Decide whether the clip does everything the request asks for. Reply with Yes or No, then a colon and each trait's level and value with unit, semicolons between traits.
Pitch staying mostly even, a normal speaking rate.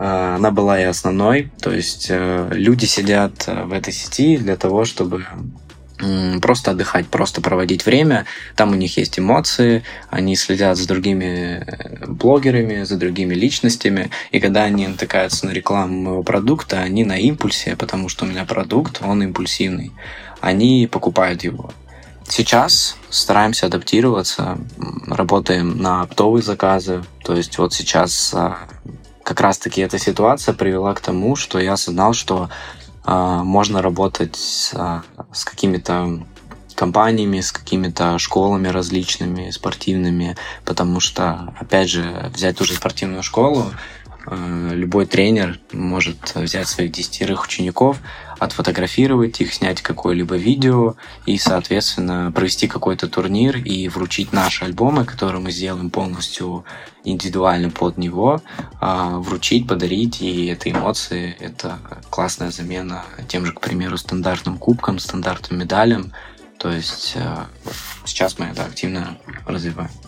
Yes: narrow, 2.2 semitones; average, 125 wpm